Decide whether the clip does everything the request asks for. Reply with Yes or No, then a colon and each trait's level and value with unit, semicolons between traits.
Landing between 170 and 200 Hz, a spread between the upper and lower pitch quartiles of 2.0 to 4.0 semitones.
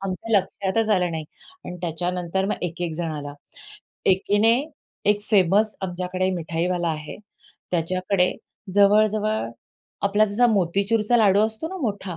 Yes: high, 190 Hz; average, 3.2 semitones